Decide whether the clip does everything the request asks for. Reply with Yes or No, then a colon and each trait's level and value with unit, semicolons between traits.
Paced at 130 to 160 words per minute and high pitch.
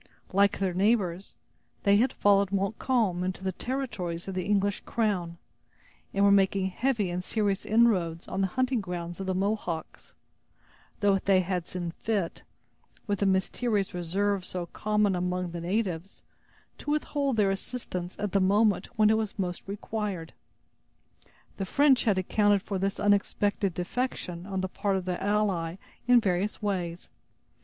Yes: average, 155 wpm; high, 195 Hz